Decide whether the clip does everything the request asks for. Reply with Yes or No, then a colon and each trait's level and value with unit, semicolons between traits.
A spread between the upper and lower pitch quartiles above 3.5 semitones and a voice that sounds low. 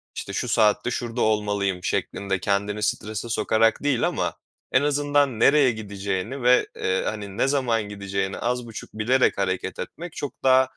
Yes: average, 4.4 semitones; low, 110 Hz